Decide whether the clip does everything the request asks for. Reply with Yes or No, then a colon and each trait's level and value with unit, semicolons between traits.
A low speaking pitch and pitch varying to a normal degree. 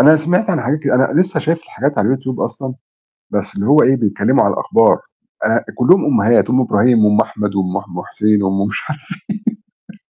No: low, 125 Hz; wide, 6.4 semitones